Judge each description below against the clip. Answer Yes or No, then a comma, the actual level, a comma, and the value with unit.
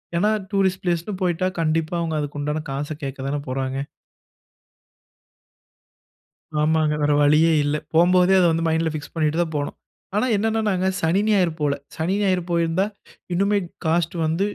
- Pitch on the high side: No, medium, 165 Hz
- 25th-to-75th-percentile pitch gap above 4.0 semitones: No, average, 3.4 semitones